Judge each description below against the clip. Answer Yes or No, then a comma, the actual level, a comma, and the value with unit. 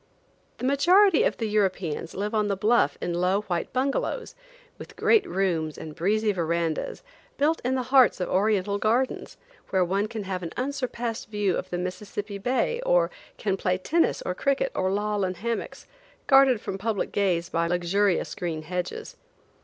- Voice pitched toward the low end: No, high, 205 Hz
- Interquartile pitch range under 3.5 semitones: No, average, 5.3 semitones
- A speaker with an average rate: Yes, average, 170 wpm